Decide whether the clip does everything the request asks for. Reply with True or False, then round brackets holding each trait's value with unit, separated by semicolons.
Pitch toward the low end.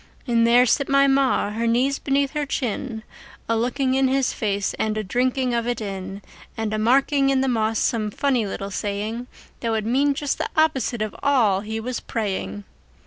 False (235 Hz)